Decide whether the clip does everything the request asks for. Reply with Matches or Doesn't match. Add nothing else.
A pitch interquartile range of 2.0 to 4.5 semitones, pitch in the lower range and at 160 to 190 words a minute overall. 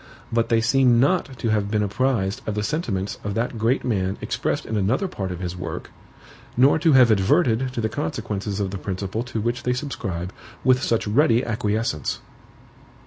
Matches